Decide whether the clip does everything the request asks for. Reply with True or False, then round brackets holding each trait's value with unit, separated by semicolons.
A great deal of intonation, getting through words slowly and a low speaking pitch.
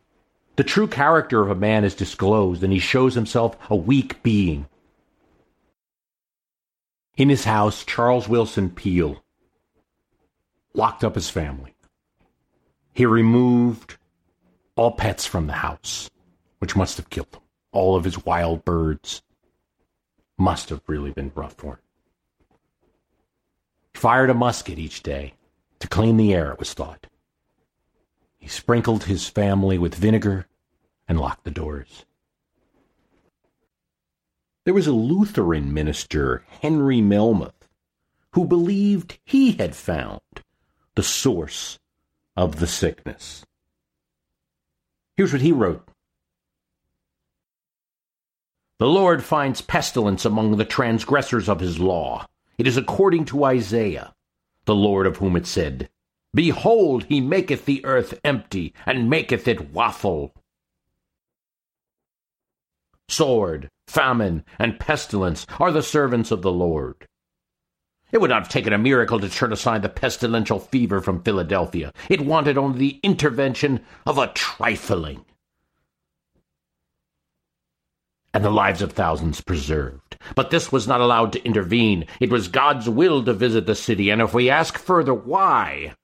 True (6.2 semitones; 130 wpm; 105 Hz)